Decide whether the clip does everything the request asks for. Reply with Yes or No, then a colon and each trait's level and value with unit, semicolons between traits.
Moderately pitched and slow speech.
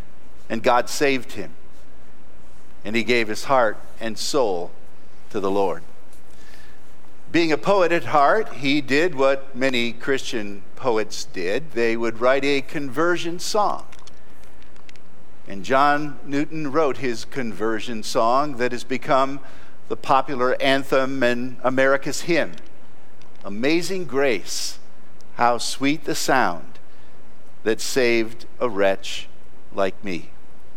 No: low, 130 Hz; slow, 115 wpm